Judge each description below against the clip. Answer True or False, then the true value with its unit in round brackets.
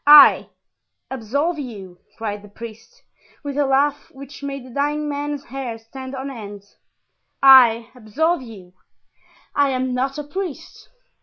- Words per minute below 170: True (140 wpm)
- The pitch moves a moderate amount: True (4.1 semitones)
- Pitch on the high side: True (265 Hz)